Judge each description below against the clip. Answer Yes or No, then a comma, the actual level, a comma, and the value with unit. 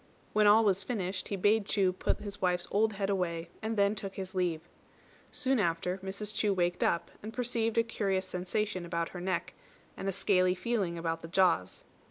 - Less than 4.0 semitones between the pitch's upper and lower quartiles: Yes, average, 2.8 semitones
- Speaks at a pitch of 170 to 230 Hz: Yes, high, 190 Hz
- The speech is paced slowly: No, average, 195 wpm